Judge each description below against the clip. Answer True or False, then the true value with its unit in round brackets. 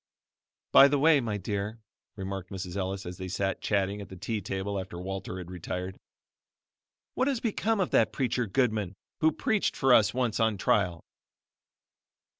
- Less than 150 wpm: False (165 wpm)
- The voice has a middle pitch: False (100 Hz)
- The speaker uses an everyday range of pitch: True (4.7 semitones)